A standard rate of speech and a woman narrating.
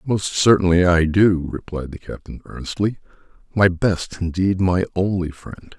No: average, 145 wpm; male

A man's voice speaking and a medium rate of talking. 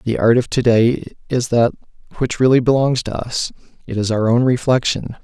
Yes: male; average, 195 wpm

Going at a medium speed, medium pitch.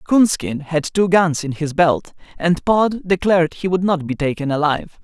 Yes: average, 190 wpm; medium, 170 Hz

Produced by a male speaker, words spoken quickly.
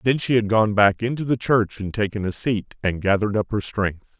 Yes: male; fast, 245 wpm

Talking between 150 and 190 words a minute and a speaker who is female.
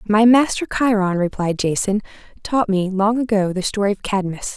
Yes: average, 170 wpm; female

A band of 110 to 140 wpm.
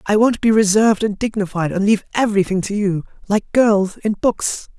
No: average, 190 wpm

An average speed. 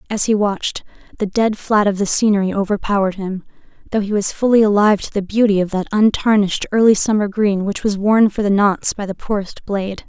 No: fast, 210 wpm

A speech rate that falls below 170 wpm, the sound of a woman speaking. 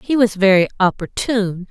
Yes: average, 140 wpm; female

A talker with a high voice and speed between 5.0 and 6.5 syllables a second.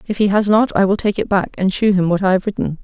Yes: high, 195 Hz; 6.4 syllables/s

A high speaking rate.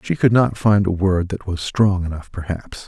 Yes: fast, 230 wpm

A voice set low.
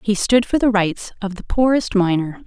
No: high, 210 Hz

